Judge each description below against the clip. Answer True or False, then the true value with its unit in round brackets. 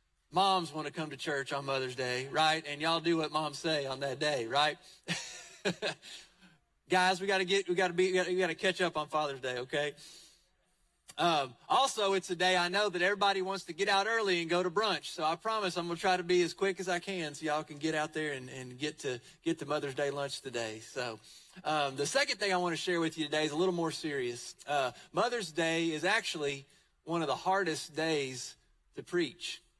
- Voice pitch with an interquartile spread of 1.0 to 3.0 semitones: False (4.1 semitones)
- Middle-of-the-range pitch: True (165 Hz)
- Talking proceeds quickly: True (230 wpm)